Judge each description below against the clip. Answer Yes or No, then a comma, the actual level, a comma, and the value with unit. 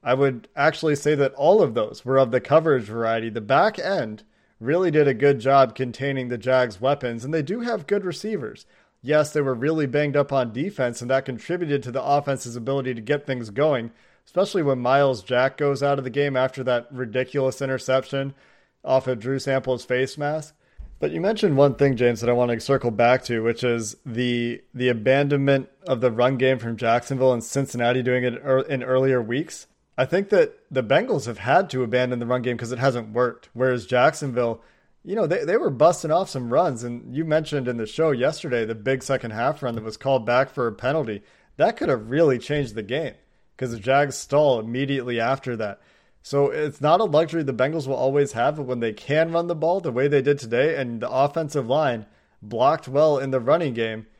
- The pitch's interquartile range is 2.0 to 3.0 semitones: Yes, narrow, 2.6 semitones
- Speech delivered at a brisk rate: Yes, fast, 215 wpm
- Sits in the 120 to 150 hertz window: Yes, low, 130 Hz